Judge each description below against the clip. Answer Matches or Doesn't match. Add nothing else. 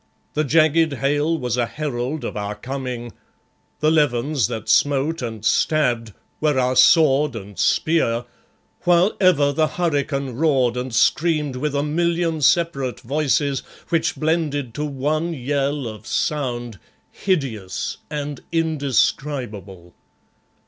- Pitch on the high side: Doesn't match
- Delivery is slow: Matches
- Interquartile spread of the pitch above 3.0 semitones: Matches